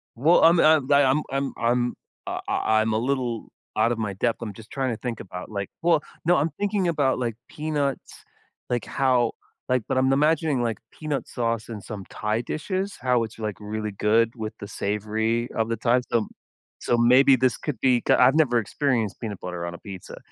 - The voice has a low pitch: Yes, low, 120 Hz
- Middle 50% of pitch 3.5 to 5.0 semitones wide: Yes, average, 4.0 semitones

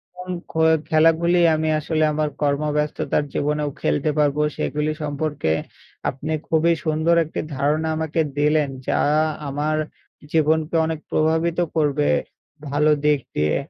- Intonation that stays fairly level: Yes, narrow, 1.4 semitones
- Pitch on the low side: No, medium, 155 Hz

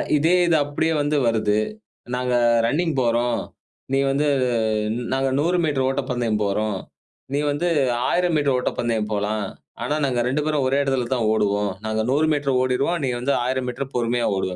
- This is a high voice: No, low, 130 Hz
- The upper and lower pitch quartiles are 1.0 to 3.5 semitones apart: No, average, 4.0 semitones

